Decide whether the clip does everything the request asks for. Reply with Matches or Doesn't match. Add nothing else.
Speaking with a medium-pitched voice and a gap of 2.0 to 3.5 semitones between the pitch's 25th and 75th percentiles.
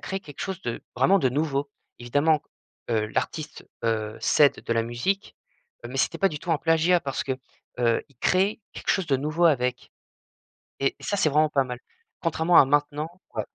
Doesn't match